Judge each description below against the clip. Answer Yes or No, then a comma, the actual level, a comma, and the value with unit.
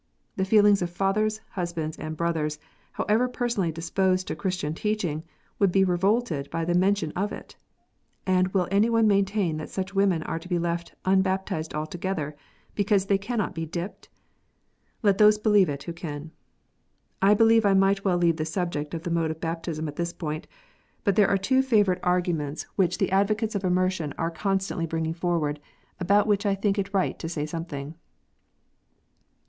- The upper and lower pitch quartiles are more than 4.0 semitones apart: No, average, 3.4 semitones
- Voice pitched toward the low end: No, medium, 185 Hz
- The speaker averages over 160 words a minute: Yes, average, 185 wpm